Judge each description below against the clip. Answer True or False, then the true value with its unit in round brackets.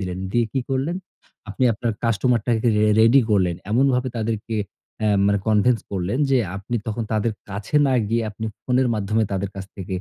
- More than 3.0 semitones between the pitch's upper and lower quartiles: True (3.5 semitones)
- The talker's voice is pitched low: True (110 Hz)